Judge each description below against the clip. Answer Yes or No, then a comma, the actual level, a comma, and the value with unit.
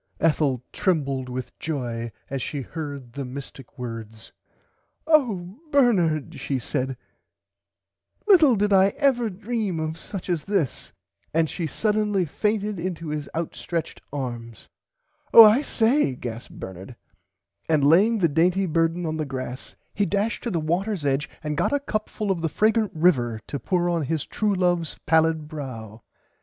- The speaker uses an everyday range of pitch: No, wide, 6.7 semitones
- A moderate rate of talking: Yes, average, 160 wpm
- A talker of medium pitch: Yes, medium, 165 Hz